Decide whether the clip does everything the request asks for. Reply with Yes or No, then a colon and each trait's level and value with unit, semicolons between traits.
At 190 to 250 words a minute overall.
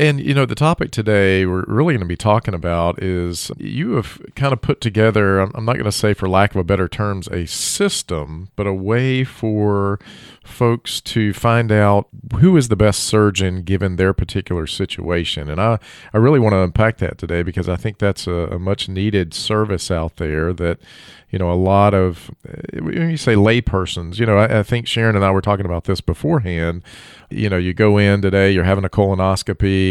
Yes: fast, 205 wpm